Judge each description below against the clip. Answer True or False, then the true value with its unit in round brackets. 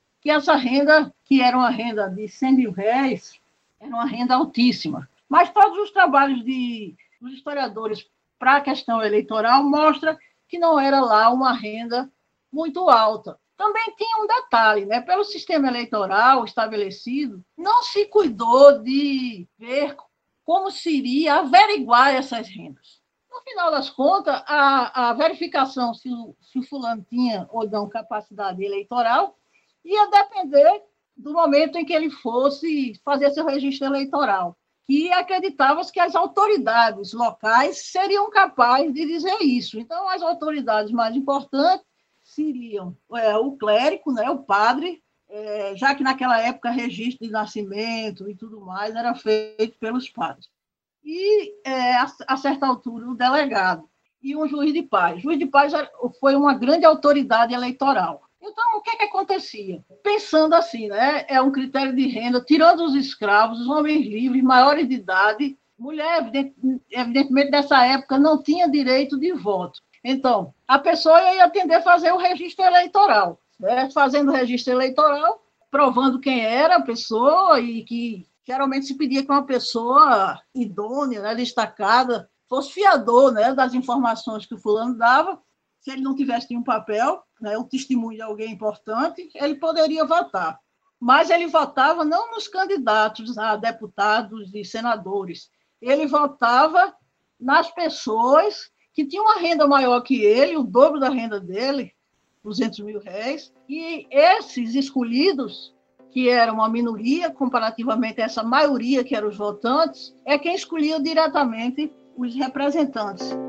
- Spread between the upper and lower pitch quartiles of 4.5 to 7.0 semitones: True (5.2 semitones)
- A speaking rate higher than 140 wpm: True (150 wpm)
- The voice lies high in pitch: True (265 Hz)